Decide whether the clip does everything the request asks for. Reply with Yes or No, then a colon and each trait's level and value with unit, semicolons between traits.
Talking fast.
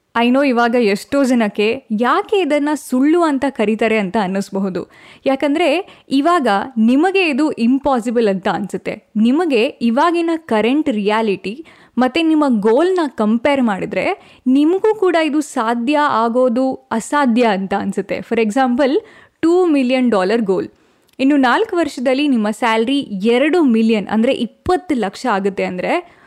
Yes: fast, 125 wpm